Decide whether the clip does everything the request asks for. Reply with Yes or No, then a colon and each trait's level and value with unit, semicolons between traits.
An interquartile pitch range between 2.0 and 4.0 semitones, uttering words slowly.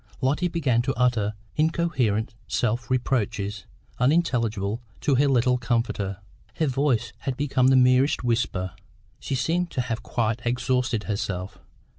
Yes: average, 3.3 semitones; slow, 130 wpm